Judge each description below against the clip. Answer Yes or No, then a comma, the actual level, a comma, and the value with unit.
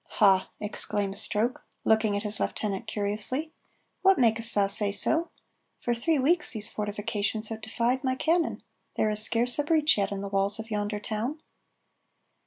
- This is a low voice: No, high, 220 Hz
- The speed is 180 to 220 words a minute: No, average, 165 wpm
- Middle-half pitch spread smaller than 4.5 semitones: Yes, average, 3.6 semitones